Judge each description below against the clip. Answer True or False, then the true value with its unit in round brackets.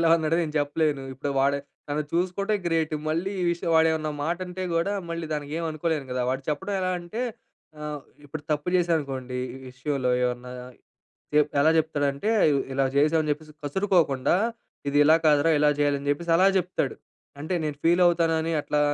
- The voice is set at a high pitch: False (155 Hz)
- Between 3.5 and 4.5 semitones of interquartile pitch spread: False (2.8 semitones)